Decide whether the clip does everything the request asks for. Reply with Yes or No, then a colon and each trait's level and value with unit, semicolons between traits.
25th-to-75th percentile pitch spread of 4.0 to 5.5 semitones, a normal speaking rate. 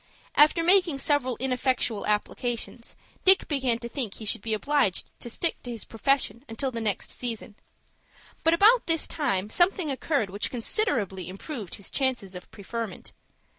Yes: average, 5.2 semitones; average, 155 wpm